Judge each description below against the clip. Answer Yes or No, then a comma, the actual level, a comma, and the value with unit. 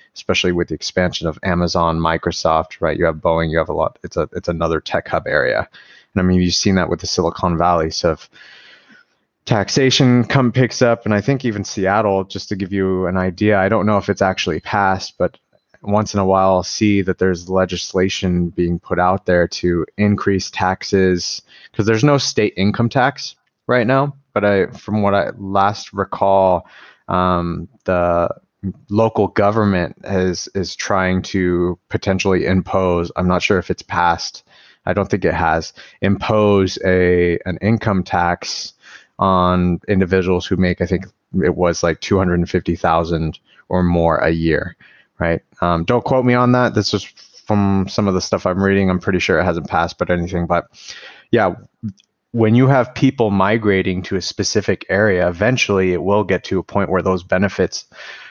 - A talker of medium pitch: No, very low, 95 Hz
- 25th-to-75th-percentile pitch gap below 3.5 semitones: Yes, narrow, 2.6 semitones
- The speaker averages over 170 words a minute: Yes, average, 180 wpm